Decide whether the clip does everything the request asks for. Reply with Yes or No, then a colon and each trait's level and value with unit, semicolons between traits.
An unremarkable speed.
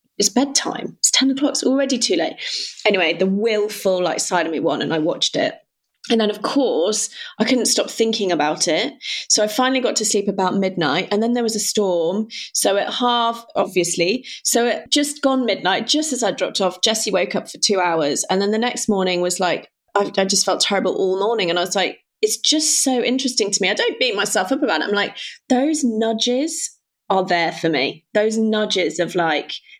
No: fast, 220 wpm